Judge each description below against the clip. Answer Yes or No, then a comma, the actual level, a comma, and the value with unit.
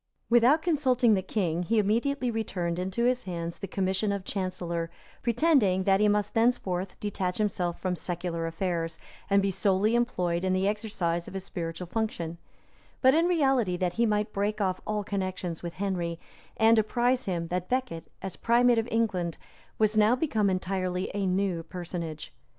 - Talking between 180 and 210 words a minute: No, average, 165 wpm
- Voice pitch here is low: No, high, 195 Hz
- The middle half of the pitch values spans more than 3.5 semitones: Yes, average, 4.0 semitones